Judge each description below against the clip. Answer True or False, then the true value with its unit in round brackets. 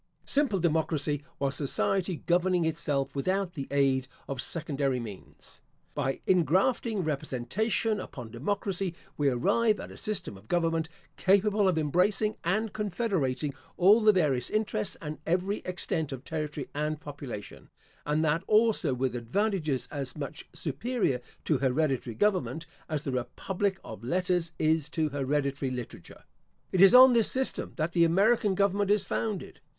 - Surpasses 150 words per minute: False (145 wpm)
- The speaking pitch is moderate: True (160 Hz)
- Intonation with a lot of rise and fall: True (6.0 semitones)